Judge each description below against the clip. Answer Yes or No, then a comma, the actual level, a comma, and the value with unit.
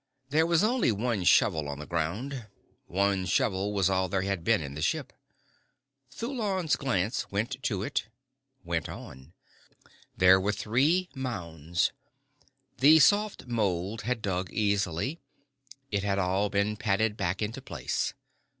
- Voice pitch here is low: Yes, low, 100 Hz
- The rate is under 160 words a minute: Yes, average, 140 wpm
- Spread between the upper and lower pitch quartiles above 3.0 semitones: Yes, wide, 5.4 semitones